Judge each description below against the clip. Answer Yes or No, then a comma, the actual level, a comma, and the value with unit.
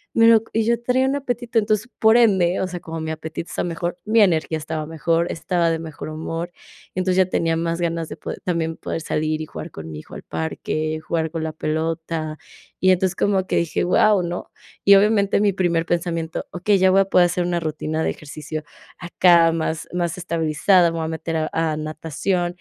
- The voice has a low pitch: No, medium, 170 Hz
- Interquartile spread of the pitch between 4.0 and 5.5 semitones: No, average, 2.8 semitones